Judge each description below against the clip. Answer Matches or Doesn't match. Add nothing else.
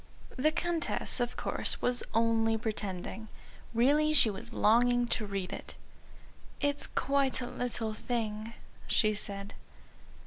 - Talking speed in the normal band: Doesn't match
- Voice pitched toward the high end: Matches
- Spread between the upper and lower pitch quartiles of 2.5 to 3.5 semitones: Matches